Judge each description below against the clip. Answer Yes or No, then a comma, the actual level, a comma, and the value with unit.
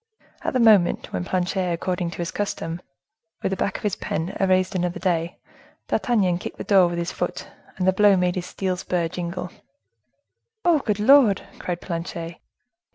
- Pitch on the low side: No, medium, 180 Hz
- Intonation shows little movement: Yes, narrow, 2.2 semitones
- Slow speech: No, average, 180 wpm